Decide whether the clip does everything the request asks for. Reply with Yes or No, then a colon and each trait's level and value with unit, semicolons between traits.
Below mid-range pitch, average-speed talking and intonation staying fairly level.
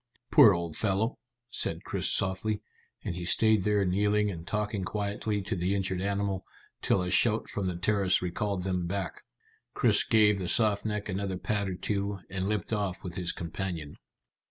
Yes: low, 100 Hz; average, 175 wpm; narrow, 2.3 semitones